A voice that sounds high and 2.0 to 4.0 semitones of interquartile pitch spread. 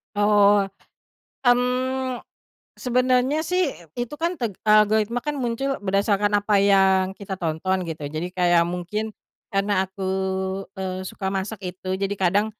No: high, 205 Hz; average, 4.4 semitones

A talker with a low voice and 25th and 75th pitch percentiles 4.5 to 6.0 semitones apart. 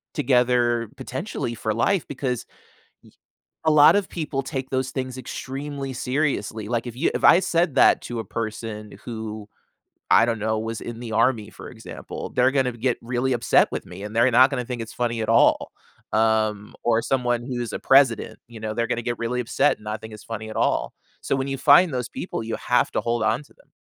No: low, 120 Hz; average, 2.9 semitones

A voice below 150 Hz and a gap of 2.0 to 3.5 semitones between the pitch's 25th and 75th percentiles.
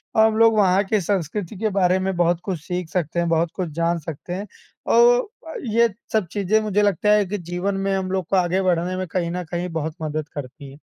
No: medium, 185 Hz; average, 3.2 semitones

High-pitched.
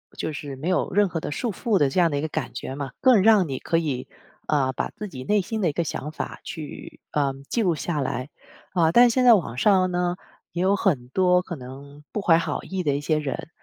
No: medium, 165 Hz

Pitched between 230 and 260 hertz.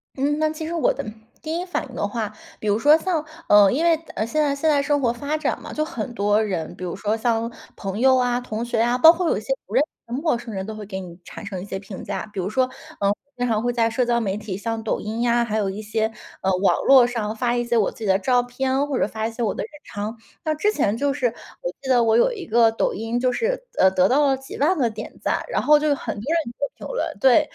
Yes: high, 240 Hz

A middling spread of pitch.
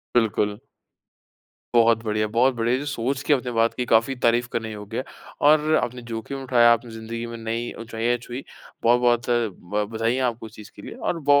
No: narrow, 1.8 semitones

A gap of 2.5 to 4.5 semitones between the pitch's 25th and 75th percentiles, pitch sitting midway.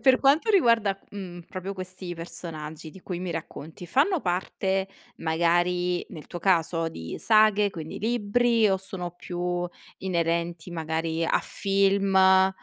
Yes: average, 2.9 semitones; medium, 180 Hz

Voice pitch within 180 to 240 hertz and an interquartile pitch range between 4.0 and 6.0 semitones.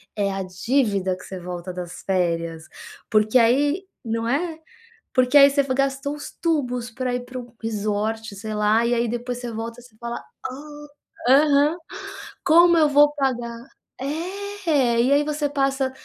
No: very high, 250 Hz; average, 4.8 semitones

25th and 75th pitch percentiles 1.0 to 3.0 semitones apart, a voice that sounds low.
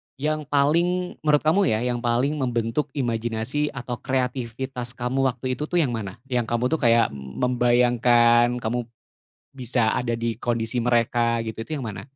Yes: narrow, 2.4 semitones; low, 120 Hz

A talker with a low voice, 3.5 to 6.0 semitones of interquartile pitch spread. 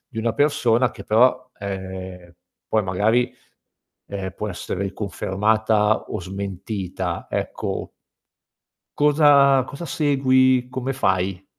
Yes: low, 110 Hz; wide, 5.4 semitones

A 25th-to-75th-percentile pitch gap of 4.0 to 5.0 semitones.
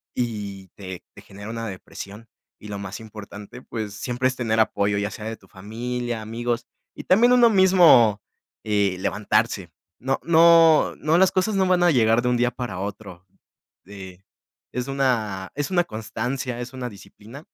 Yes: average, 4.6 semitones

